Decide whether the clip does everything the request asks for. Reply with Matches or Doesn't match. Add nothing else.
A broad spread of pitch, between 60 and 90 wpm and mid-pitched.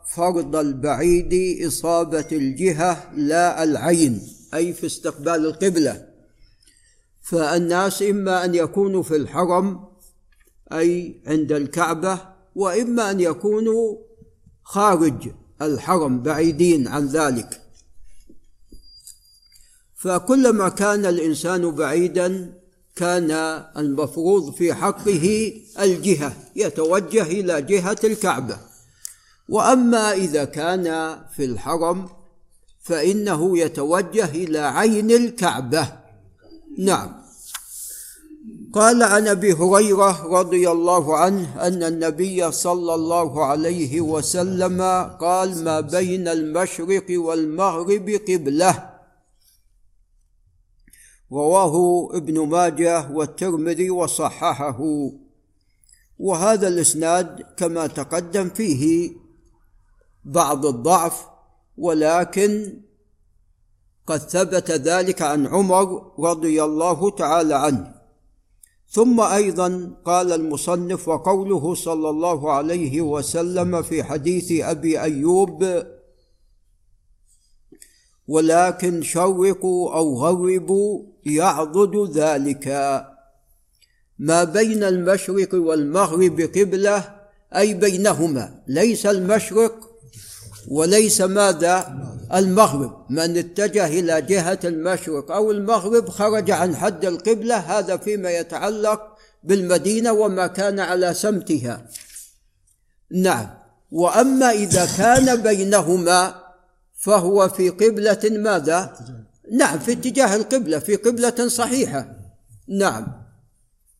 Doesn't match